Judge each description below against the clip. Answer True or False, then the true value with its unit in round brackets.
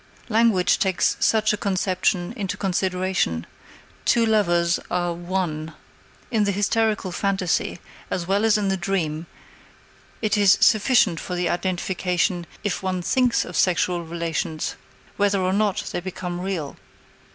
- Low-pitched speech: False (185 Hz)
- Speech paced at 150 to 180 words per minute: False (135 wpm)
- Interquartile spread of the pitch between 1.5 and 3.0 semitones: True (2.7 semitones)